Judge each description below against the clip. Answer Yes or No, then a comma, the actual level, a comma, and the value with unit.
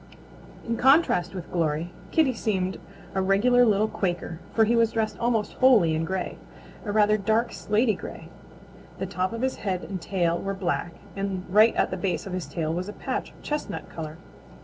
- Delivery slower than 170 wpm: No, average, 190 wpm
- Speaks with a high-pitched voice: Yes, high, 195 Hz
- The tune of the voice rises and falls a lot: No, average, 4.0 semitones